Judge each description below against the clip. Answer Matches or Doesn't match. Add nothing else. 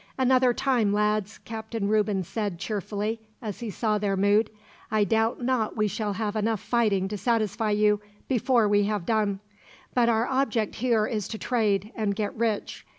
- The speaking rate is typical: Matches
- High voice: Matches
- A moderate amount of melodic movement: Doesn't match